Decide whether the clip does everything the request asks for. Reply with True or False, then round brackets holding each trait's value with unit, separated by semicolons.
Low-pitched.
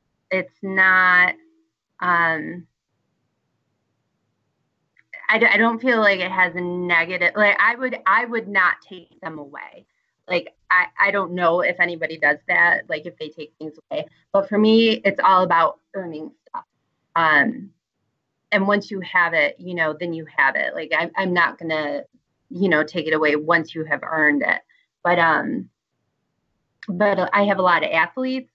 False (180 Hz)